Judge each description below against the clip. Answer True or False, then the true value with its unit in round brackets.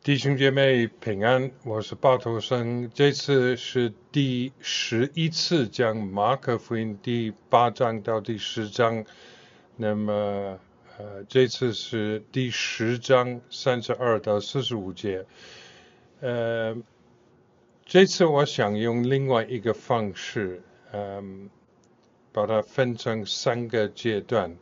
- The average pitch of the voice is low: True (120 Hz)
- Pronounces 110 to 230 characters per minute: True (170 characters per minute)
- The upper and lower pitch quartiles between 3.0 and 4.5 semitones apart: True (3.3 semitones)